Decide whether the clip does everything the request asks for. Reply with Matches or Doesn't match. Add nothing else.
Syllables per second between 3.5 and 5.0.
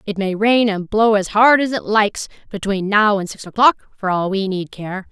Matches